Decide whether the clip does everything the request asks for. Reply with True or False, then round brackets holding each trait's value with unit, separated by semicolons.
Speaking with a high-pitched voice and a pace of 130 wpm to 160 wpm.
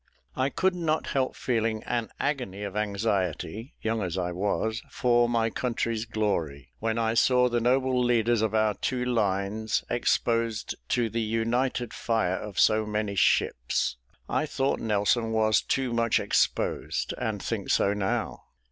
False (115 Hz; 150 wpm)